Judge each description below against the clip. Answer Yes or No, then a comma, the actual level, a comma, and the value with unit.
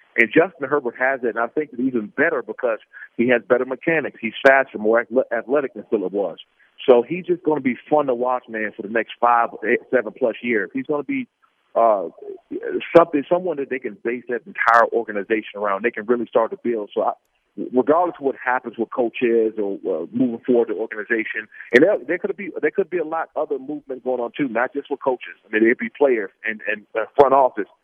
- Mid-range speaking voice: No, low, 130 Hz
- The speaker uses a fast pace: Yes, fast, 230 wpm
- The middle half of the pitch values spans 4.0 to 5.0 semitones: Yes, average, 4.5 semitones